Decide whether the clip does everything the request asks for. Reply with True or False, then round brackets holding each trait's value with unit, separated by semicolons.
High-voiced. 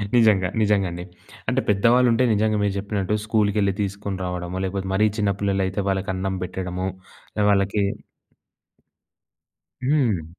False (100 Hz)